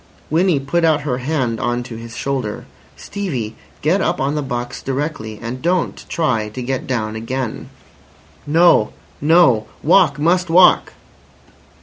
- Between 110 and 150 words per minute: Yes, average, 140 wpm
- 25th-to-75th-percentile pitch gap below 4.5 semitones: No, average, 5.2 semitones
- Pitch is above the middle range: No, low, 135 Hz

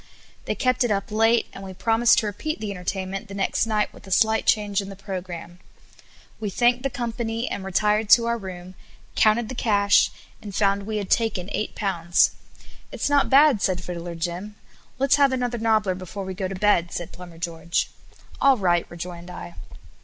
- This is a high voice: Yes, high, 205 Hz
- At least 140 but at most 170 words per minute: No, average, 190 wpm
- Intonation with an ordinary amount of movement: Yes, average, 3.6 semitones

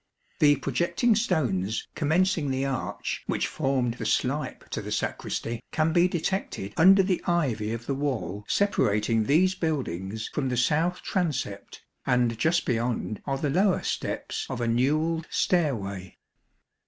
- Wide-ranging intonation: Yes, wide, 6.4 semitones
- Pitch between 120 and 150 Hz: Yes, medium, 140 Hz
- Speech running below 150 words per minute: Yes, average, 140 wpm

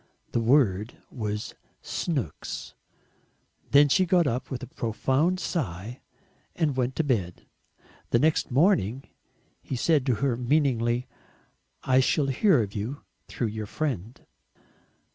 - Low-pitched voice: Yes, low, 130 Hz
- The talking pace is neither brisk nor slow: No, slow, 125 wpm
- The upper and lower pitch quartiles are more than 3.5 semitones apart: Yes, average, 4.3 semitones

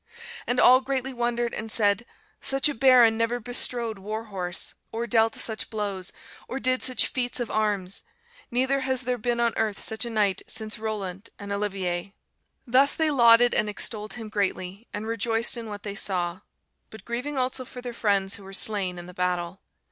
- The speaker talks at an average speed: Yes, average, 185 wpm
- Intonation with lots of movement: No, average, 3.3 semitones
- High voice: Yes, high, 220 Hz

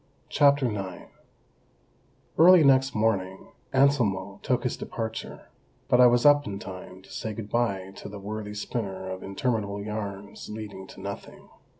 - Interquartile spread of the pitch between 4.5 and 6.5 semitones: No, average, 3.9 semitones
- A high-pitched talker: No, low, 105 Hz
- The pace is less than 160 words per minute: Yes, average, 145 wpm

